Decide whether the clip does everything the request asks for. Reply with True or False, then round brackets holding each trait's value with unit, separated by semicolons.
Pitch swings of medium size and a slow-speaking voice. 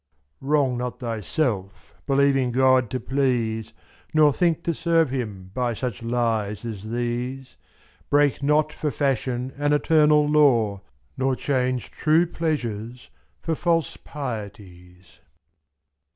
True (4.3 semitones; 115 wpm)